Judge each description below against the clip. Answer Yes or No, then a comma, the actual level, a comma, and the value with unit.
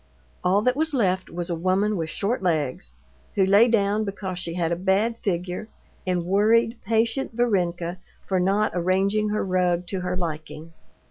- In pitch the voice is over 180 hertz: Yes, high, 190 Hz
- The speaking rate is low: No, average, 165 wpm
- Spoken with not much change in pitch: No, average, 3.3 semitones